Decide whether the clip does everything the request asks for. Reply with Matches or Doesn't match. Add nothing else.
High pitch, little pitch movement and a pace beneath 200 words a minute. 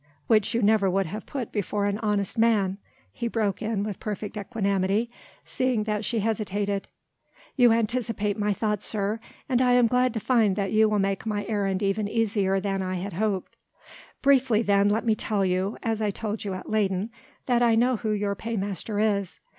Matches